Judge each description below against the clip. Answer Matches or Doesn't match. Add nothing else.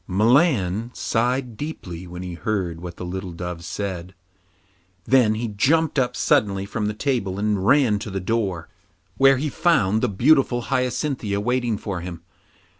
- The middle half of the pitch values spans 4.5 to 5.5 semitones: Matches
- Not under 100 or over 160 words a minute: Matches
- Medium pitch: Doesn't match